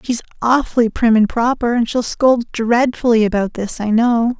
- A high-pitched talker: Yes, high, 235 Hz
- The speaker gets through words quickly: No, average, 175 wpm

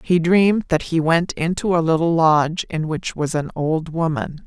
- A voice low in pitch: No, medium, 165 Hz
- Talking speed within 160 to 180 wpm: No, average, 200 wpm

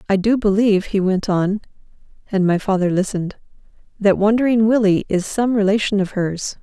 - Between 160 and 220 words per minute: Yes, average, 165 wpm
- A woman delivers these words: Yes, female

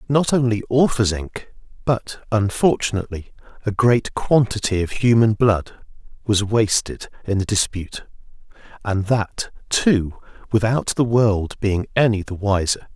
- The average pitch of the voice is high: No, low, 110 Hz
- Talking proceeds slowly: Yes, slow, 125 wpm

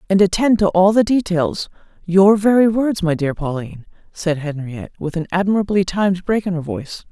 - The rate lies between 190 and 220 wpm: No, average, 175 wpm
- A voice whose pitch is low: No, medium, 185 Hz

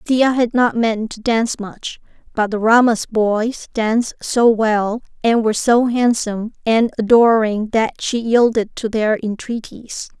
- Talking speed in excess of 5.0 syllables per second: No, 4.1 syllables/s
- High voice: Yes, high, 225 Hz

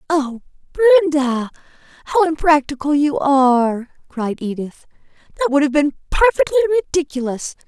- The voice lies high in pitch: Yes, very high, 300 Hz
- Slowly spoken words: Yes, slow, 110 wpm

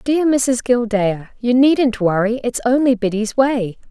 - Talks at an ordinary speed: Yes, average, 155 wpm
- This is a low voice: No, high, 235 Hz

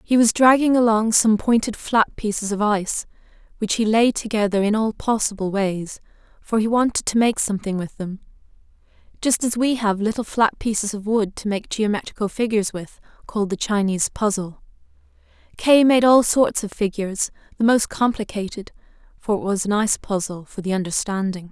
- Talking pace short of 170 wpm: No, average, 175 wpm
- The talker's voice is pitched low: No, high, 210 Hz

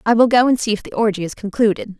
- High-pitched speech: Yes, high, 215 Hz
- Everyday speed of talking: No, fast, 300 wpm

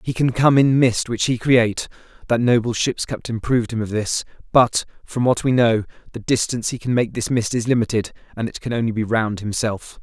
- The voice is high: No, low, 115 Hz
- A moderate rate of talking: No, fast, 215 wpm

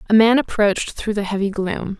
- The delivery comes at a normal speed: No, fast, 210 wpm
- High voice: Yes, high, 210 Hz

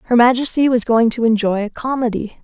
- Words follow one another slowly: No, average, 195 wpm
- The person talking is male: No, female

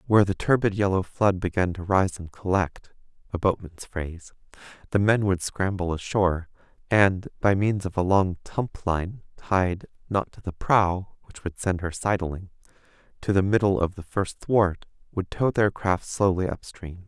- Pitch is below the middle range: Yes, very low, 95 Hz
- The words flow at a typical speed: Yes, average, 160 wpm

